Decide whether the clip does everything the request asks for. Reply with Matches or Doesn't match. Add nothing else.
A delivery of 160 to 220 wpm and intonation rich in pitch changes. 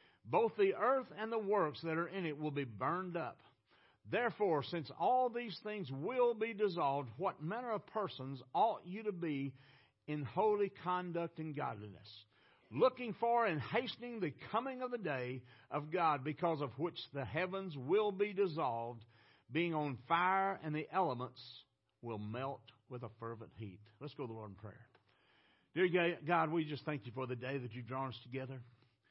Matches